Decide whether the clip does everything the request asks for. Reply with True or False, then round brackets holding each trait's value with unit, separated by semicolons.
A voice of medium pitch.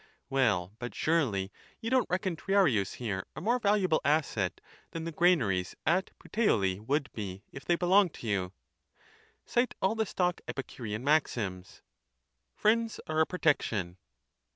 True (150 Hz)